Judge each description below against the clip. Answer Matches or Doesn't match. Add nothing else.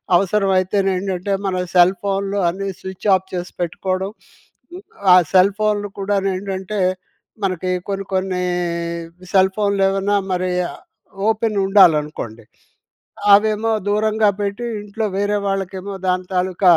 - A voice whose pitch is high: Matches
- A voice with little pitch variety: Matches